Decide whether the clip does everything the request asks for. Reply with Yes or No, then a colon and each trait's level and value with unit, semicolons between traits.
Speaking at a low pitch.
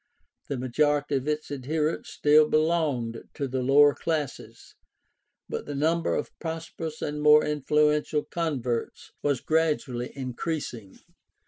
No: medium, 150 Hz